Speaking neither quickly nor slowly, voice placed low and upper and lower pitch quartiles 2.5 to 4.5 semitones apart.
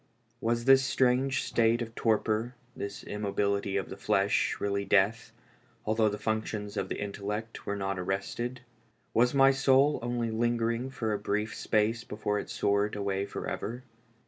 Yes: average, 165 wpm; low, 110 Hz; average, 2.8 semitones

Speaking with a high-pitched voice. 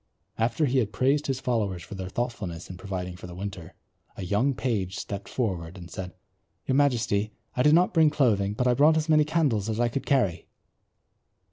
No: low, 110 Hz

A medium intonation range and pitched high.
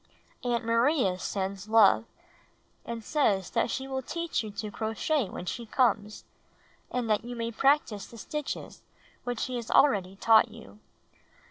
Yes: average, 3.3 semitones; high, 230 Hz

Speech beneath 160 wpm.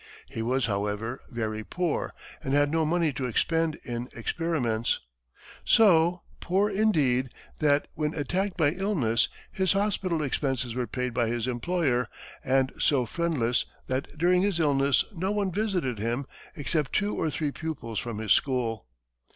Yes: average, 150 wpm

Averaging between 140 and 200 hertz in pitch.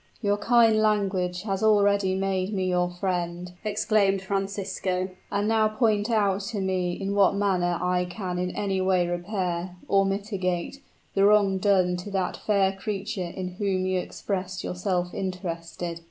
Yes: high, 190 Hz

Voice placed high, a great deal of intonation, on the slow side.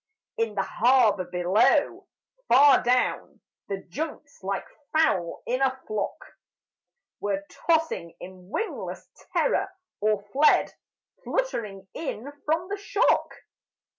Yes: high, 230 Hz; wide, 7.7 semitones; slow, 105 wpm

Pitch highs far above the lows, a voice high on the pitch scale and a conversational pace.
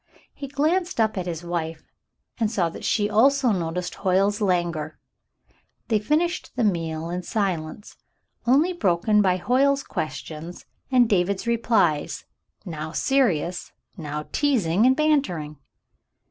No: wide, 6.8 semitones; high, 195 Hz; slow, 130 wpm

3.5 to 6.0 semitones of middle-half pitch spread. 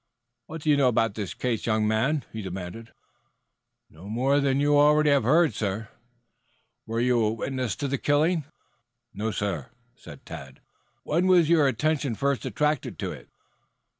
Yes: average, 5.2 semitones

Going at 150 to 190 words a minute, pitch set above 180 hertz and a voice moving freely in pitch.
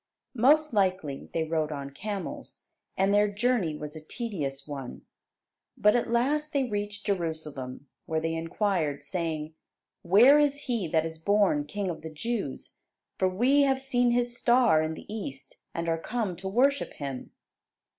Yes: average, 160 wpm; high, 190 Hz; wide, 7.2 semitones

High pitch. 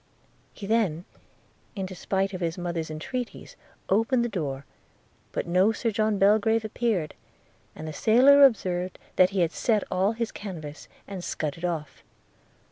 Yes: high, 195 Hz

